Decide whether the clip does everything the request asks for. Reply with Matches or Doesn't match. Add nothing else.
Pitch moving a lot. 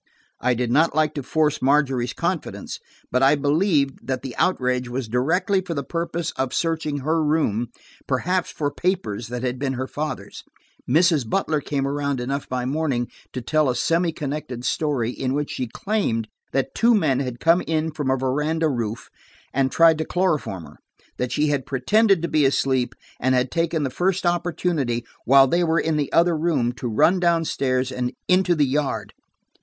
Doesn't match